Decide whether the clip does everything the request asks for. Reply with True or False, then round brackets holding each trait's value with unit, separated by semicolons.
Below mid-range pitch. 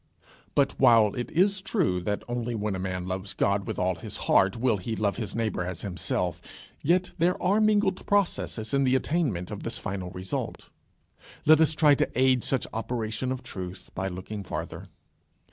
True (110 Hz)